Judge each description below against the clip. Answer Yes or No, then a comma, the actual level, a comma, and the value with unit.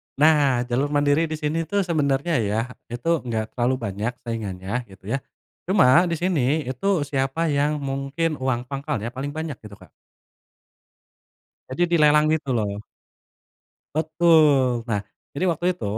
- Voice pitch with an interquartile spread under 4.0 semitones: No, average, 4.6 semitones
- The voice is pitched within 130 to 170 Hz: Yes, medium, 140 Hz